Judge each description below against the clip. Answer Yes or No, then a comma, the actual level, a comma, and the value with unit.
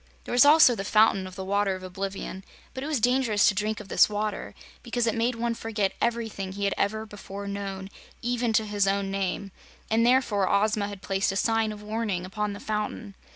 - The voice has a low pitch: No, high, 210 Hz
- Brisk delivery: Yes, fast, 210 wpm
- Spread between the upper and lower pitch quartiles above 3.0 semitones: No, narrow, 2.5 semitones